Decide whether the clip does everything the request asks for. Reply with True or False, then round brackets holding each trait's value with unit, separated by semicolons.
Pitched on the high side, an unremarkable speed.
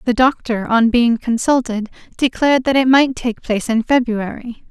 True (240 Hz; 165 wpm)